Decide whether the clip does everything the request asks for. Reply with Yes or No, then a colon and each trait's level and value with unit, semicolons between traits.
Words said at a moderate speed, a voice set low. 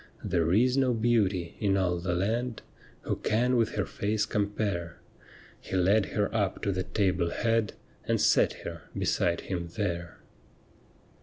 Yes: average, 150 wpm; low, 100 Hz